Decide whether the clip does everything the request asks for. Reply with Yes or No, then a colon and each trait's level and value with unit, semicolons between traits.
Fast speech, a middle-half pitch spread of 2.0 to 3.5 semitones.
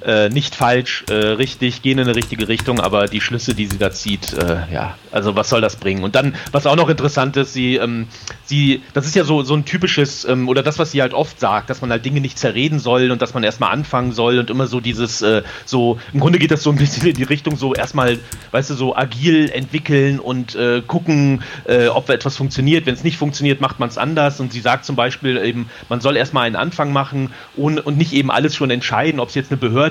Yes: fast, 250 wpm; average, 3.1 semitones